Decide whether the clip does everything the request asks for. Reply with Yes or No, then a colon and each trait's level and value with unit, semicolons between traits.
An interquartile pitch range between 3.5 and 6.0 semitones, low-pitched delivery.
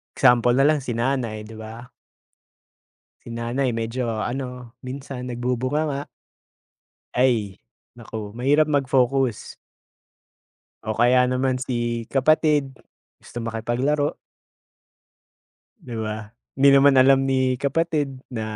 No: average, 2.7 semitones; low, 125 Hz